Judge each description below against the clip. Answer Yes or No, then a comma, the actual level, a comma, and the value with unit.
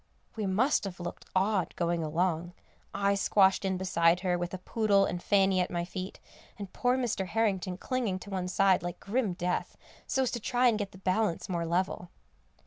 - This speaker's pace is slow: No, average, 195 wpm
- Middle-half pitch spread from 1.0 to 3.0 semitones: Yes, narrow, 2.6 semitones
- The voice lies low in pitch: No, high, 190 Hz